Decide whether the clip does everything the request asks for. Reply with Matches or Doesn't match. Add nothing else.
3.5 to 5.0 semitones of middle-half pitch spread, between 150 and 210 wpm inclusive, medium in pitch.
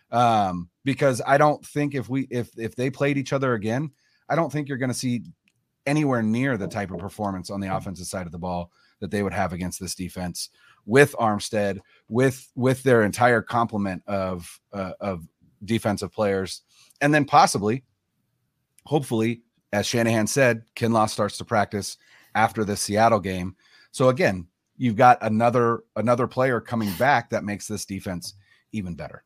Doesn't match